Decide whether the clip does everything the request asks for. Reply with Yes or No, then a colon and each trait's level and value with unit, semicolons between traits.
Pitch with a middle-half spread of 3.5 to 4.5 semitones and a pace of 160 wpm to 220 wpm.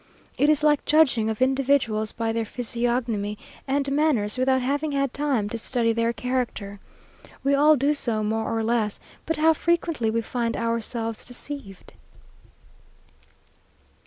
No: average, 4.0 semitones; average, 140 wpm